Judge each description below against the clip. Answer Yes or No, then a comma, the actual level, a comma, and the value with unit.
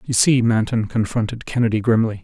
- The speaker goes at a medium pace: Yes, average, 160 wpm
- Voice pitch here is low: Yes, low, 115 Hz